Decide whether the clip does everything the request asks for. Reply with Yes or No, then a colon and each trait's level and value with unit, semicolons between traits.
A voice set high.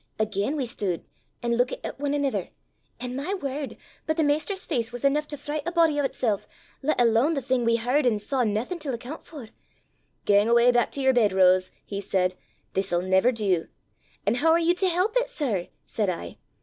Yes: very high, 250 Hz